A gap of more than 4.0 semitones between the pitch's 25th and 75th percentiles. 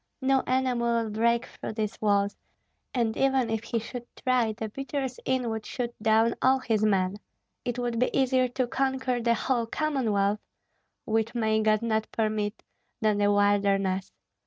No: average, 2.9 semitones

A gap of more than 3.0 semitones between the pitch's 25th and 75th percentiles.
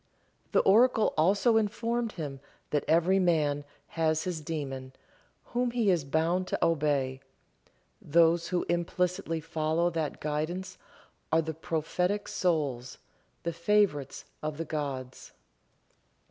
Yes: average, 3.5 semitones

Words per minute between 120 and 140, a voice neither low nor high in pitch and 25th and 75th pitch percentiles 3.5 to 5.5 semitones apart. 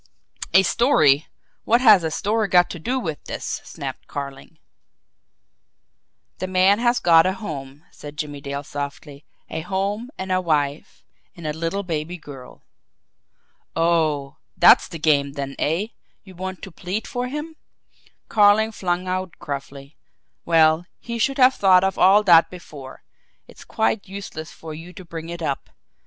No: average, 155 wpm; medium, 170 Hz; average, 4.7 semitones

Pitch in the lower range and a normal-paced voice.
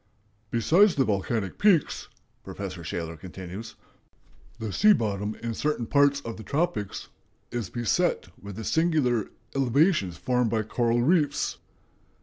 No: low, 115 Hz; slow, 130 wpm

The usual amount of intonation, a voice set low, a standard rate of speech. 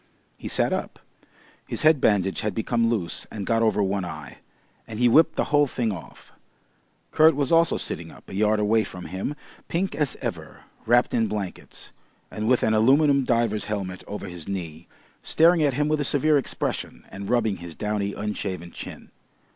No: wide, 5.8 semitones; low, 110 Hz; average, 180 wpm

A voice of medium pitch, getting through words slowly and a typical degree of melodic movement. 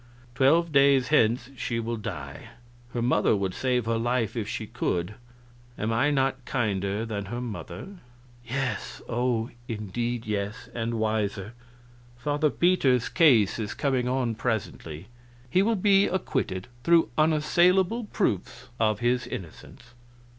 No: low, 120 Hz; slow, 130 wpm; average, 4.2 semitones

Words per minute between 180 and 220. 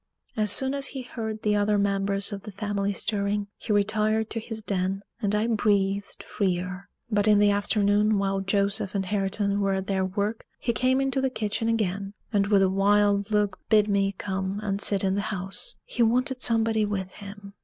Yes: average, 195 wpm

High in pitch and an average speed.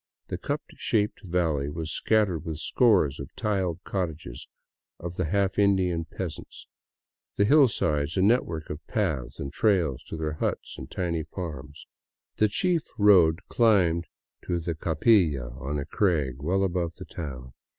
No: very low, 85 Hz; average, 150 wpm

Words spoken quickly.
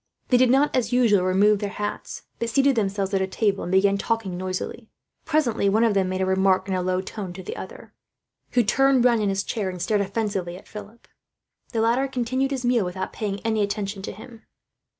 Yes: fast, 210 wpm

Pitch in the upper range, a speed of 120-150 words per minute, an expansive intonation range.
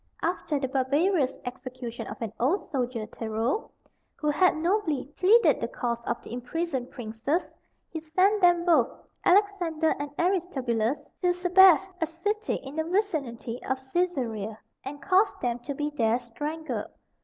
Yes: very high, 300 Hz; average, 145 wpm; wide, 6.4 semitones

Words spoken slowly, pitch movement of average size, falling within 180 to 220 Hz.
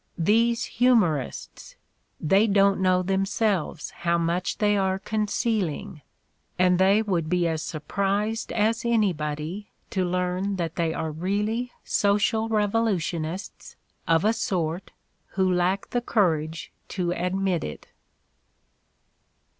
Yes: slow, 115 wpm; average, 3.5 semitones; high, 190 Hz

